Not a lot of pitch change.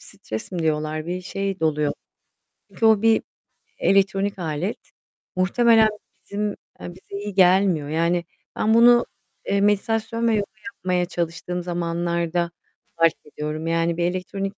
No: average, 3.3 semitones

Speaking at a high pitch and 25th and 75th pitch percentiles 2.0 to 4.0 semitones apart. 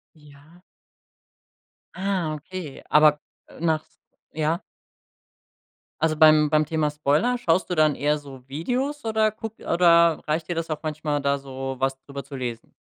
No: medium, 155 Hz; average, 2.8 semitones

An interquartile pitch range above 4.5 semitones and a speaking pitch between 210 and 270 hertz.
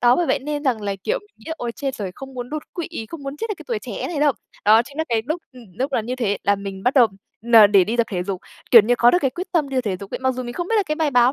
Yes: average, 5.1 semitones; very high, 255 Hz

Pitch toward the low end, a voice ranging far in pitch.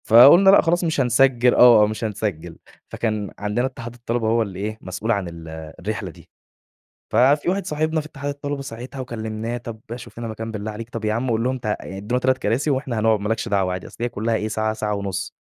No: low, 115 Hz; average, 3.4 semitones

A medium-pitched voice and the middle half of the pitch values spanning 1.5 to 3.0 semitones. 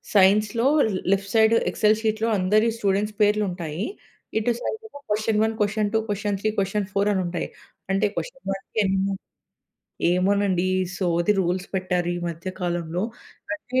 No: high, 200 Hz; narrow, 2.5 semitones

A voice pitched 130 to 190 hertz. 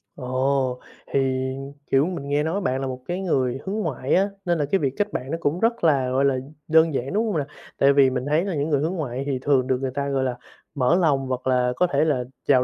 Yes: medium, 140 Hz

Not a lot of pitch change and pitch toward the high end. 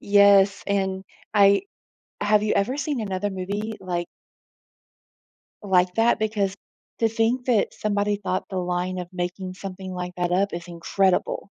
Yes: narrow, 2.3 semitones; high, 195 Hz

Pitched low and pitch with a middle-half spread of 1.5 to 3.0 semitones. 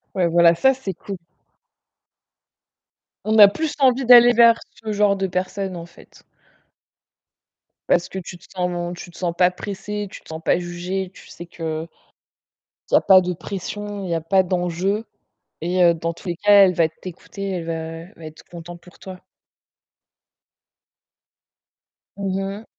No: medium, 185 Hz; narrow, 2.6 semitones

